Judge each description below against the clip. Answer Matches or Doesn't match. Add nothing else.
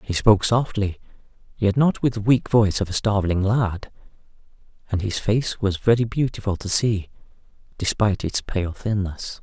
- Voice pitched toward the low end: Matches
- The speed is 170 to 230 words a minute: Doesn't match